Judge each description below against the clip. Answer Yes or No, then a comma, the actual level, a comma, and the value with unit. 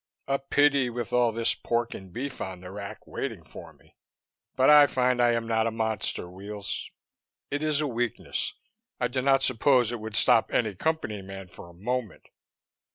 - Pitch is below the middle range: Yes, low, 120 Hz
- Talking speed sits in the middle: Yes, average, 185 wpm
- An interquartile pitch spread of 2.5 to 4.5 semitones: Yes, average, 4.0 semitones